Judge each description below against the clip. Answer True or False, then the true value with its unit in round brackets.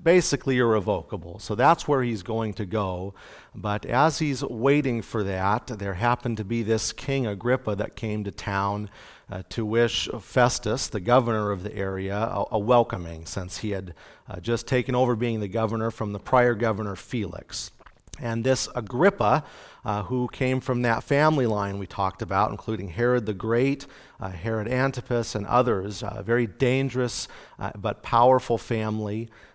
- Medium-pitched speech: False (115 Hz)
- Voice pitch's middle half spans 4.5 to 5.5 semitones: False (3.3 semitones)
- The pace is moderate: True (170 wpm)